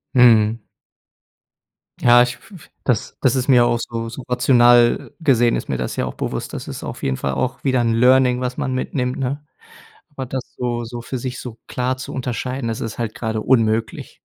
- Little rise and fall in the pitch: Yes, narrow, 2.0 semitones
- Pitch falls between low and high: No, low, 125 Hz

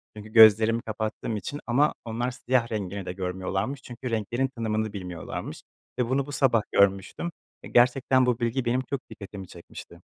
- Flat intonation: No, average, 3.7 semitones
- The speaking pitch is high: No, low, 115 Hz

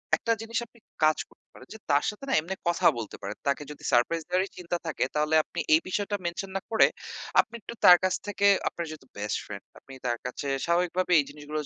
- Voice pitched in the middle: Yes, medium, 170 Hz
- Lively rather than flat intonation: No, average, 4.7 semitones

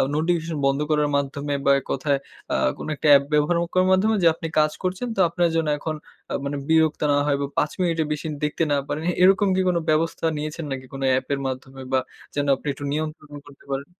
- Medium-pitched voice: Yes, medium, 150 Hz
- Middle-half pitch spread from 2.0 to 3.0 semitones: Yes, average, 2.7 semitones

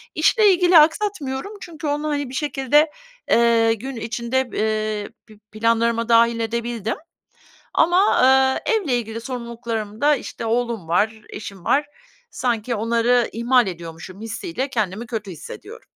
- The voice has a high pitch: Yes, high, 235 Hz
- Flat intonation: No, average, 3.4 semitones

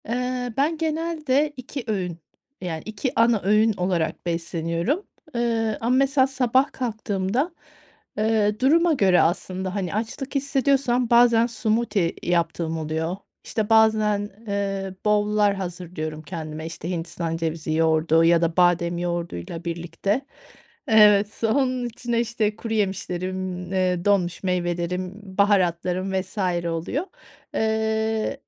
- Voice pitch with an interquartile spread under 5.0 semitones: No, average, 5.3 semitones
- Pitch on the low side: No, high, 205 Hz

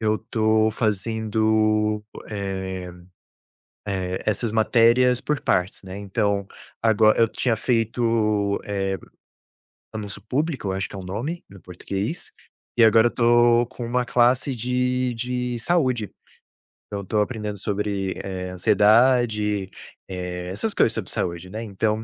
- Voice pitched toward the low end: Yes, low, 110 Hz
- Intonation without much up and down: No, average, 3.2 semitones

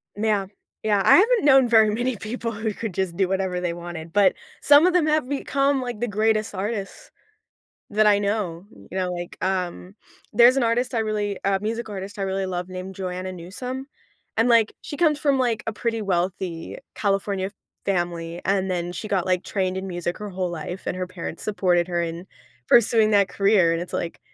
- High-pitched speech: Yes, high, 200 Hz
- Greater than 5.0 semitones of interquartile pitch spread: No, average, 3.8 semitones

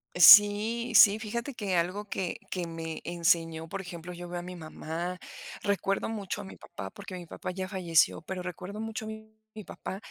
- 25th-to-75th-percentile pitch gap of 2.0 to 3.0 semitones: No, average, 3.5 semitones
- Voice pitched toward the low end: No, medium, 185 Hz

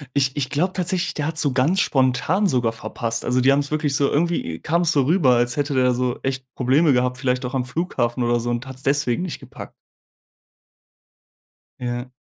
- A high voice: No, low, 135 Hz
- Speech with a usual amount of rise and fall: Yes, average, 3.4 semitones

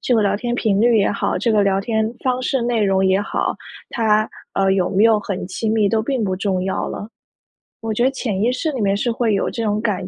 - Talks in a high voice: Yes, high, 215 Hz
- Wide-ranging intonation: No, average, 3.0 semitones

